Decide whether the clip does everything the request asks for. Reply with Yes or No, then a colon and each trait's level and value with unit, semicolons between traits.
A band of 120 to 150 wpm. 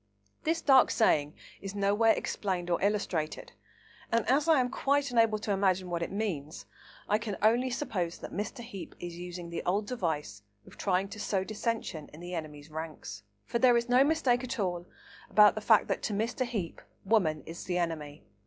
No: average, 190 wpm